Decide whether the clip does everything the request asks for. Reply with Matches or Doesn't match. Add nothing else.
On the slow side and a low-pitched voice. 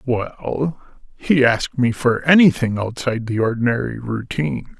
Matches